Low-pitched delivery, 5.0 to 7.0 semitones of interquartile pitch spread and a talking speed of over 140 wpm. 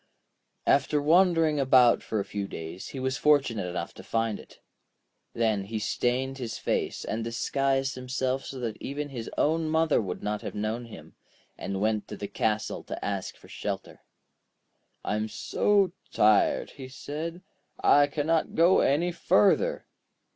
Yes: low, 130 Hz; wide, 5.5 semitones; average, 155 wpm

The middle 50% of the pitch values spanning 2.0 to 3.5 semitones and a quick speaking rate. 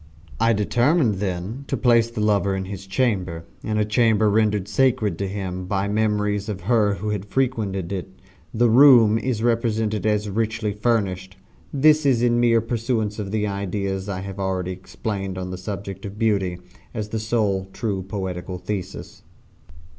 No: average, 2.9 semitones; average, 160 wpm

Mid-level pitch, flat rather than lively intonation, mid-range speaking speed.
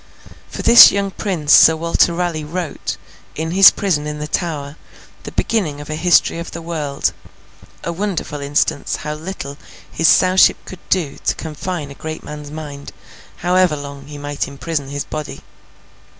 No: medium, 155 Hz; average, 3.3 semitones; average, 165 wpm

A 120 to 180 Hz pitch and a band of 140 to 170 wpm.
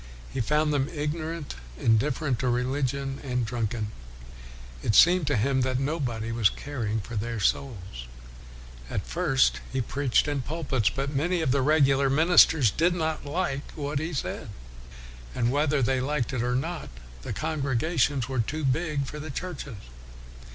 Yes: low, 135 Hz; average, 160 wpm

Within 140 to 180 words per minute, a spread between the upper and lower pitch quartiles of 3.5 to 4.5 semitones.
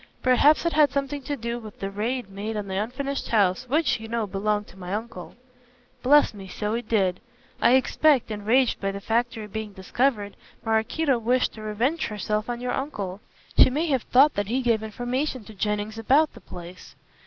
No: average, 190 wpm; average, 4.0 semitones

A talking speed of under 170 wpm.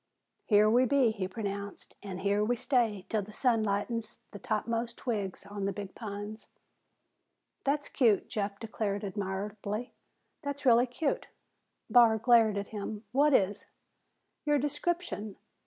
Yes: average, 140 wpm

